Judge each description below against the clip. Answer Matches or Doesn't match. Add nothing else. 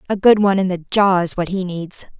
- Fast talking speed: Matches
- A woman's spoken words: Matches